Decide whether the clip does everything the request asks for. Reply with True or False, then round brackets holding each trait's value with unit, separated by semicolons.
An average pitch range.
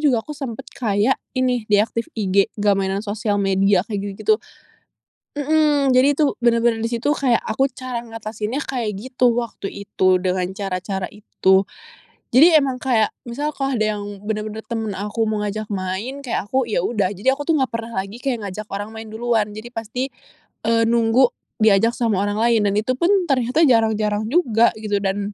True (3.6 semitones)